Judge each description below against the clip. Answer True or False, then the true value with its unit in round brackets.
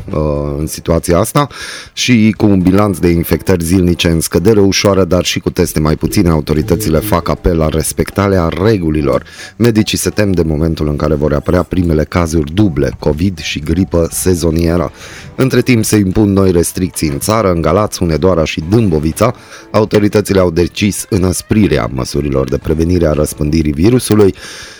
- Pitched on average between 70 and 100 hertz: True (90 Hz)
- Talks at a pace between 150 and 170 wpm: True (155 wpm)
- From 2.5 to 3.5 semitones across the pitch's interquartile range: False (4.3 semitones)